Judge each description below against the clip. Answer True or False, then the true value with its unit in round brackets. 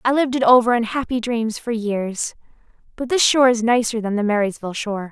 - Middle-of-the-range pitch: False (230 Hz)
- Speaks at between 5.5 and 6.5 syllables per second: True (6.2 syllables/s)